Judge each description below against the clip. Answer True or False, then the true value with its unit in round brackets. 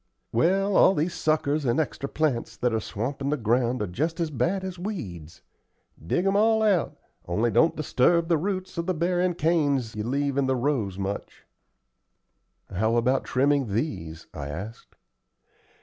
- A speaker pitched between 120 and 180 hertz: True (140 Hz)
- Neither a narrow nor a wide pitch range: False (6.8 semitones)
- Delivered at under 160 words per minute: False (165 wpm)